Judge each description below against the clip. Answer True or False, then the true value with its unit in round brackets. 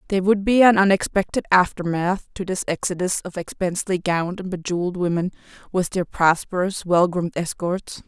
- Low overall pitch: False (180 Hz)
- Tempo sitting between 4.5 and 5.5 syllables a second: False (5.8 syllables/s)